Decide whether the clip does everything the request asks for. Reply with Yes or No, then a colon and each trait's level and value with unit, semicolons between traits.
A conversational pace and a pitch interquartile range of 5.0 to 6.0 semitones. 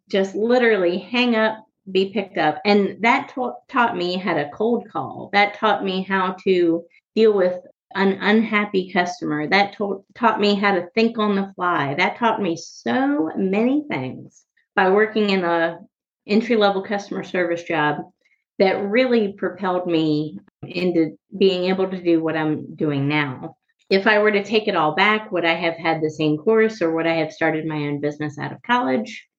No: average, 185 wpm; average, 4.3 semitones